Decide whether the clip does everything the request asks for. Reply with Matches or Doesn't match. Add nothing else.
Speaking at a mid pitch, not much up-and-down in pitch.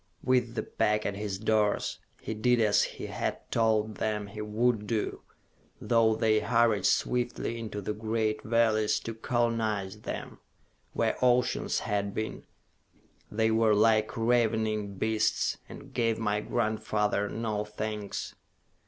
Doesn't match